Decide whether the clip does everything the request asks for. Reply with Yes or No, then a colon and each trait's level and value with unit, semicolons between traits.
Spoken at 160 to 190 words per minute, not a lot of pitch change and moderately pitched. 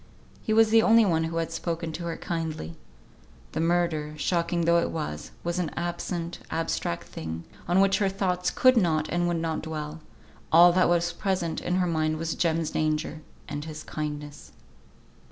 Yes: average, 175 wpm; narrow, 2.0 semitones; medium, 165 Hz